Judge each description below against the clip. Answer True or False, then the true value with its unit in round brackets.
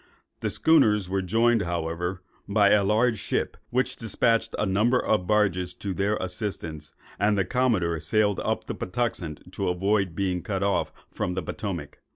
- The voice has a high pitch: False (100 Hz)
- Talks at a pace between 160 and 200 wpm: True (165 wpm)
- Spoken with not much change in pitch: False (3.2 semitones)